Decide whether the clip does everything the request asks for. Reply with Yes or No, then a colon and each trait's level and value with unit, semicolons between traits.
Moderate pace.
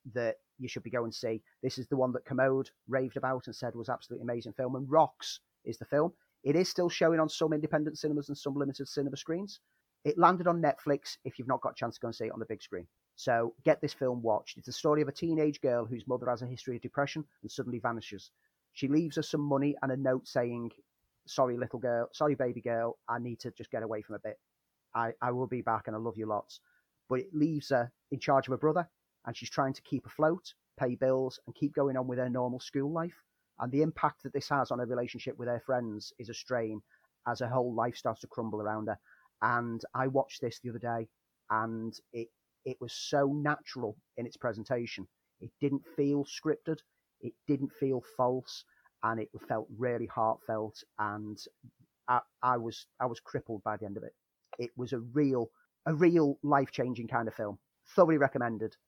No: fast, 220 wpm